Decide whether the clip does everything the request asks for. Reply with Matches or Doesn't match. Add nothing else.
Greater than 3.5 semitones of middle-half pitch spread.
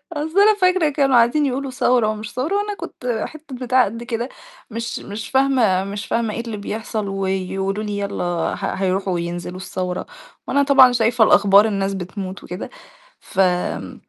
Matches